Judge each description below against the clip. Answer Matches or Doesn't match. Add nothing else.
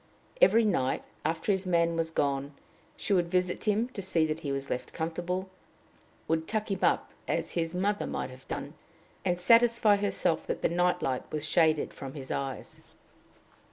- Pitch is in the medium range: Matches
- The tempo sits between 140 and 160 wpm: Doesn't match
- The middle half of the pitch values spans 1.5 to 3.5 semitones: Doesn't match